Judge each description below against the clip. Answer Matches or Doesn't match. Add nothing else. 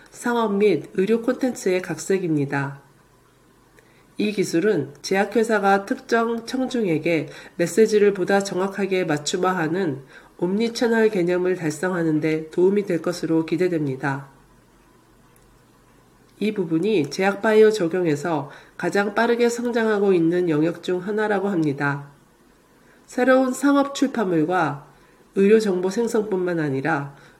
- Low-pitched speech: Doesn't match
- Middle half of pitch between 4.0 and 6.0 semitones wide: Matches